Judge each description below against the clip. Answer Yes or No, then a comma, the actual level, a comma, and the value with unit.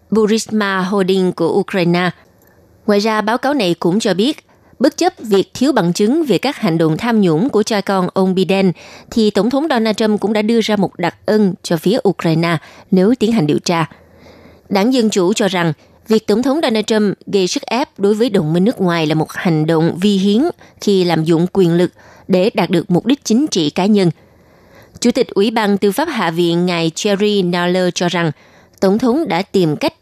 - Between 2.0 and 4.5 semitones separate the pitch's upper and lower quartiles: Yes, average, 3.9 semitones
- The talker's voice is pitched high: Yes, high, 195 Hz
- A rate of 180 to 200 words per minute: No, average, 210 wpm